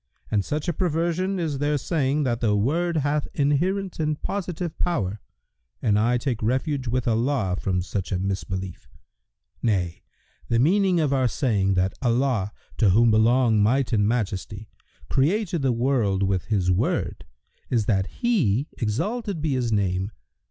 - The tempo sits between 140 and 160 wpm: Yes, average, 155 wpm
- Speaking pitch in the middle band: No, low, 125 Hz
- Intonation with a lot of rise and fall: Yes, wide, 6.7 semitones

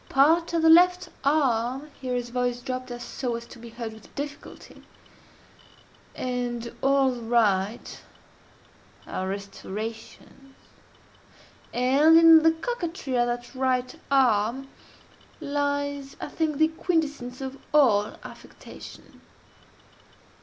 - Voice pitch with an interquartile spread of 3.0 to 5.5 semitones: Yes, average, 3.6 semitones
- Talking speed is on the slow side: Yes, slow, 110 wpm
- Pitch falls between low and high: No, very high, 260 Hz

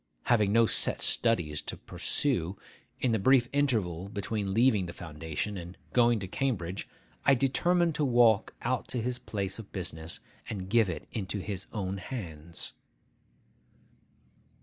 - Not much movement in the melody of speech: No, average, 4.9 semitones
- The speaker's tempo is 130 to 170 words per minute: Yes, average, 145 wpm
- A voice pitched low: Yes, low, 105 Hz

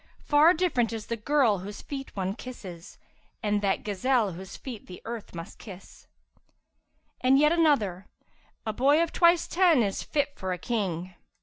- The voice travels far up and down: Yes, wide, 6.9 semitones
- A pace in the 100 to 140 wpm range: No, average, 170 wpm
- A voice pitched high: Yes, high, 225 Hz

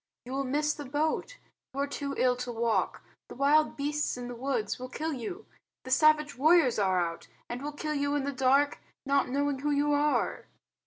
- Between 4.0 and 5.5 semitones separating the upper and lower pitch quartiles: No, average, 2.7 semitones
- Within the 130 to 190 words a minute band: No, fast, 205 wpm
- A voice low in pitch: No, very high, 280 Hz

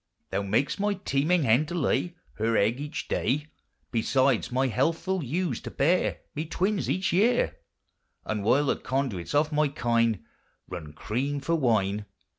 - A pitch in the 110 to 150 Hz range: Yes, medium, 140 Hz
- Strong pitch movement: Yes, wide, 6.5 semitones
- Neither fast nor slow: Yes, average, 155 wpm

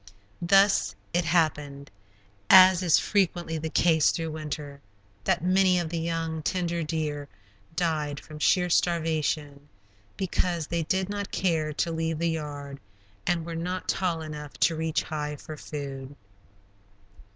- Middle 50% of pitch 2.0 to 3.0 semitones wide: Yes, narrow, 2.5 semitones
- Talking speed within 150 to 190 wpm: No, average, 140 wpm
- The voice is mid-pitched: Yes, medium, 160 Hz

